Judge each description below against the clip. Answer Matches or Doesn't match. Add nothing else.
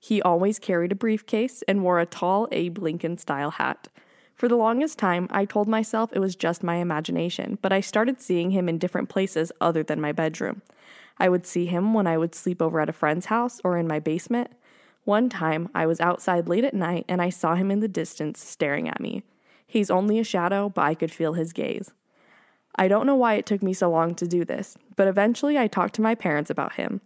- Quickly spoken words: Matches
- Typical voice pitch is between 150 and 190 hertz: Matches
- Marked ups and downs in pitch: Doesn't match